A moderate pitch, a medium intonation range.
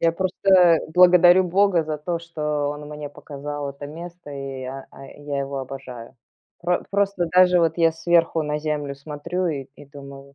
Yes: medium, 150 Hz; average, 3.7 semitones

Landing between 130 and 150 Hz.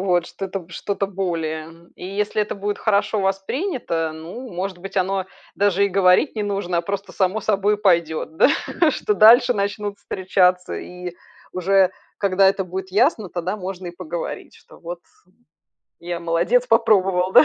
No: high, 190 Hz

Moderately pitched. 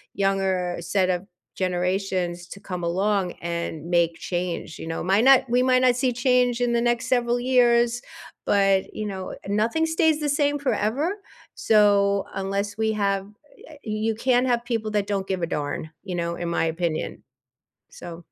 No: high, 200 Hz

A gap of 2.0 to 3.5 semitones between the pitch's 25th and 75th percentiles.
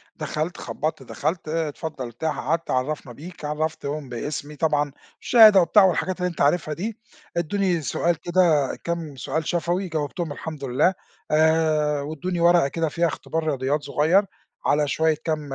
Yes: average, 2.7 semitones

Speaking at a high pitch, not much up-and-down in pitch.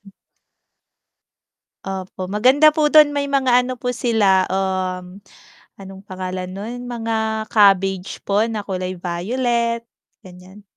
No: high, 205 Hz; average, 4.5 semitones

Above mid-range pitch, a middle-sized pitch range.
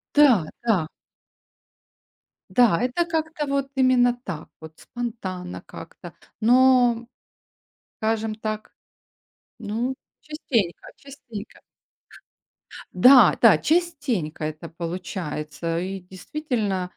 No: high, 225 Hz; wide, 6.4 semitones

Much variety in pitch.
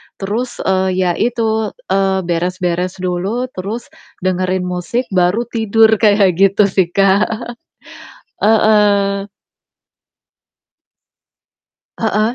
No: average, 3.1 semitones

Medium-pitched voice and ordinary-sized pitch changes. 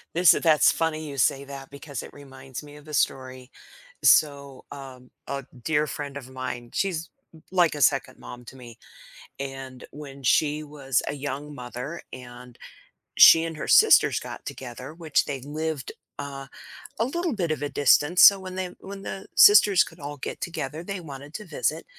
Yes: medium, 145 Hz; average, 3.1 semitones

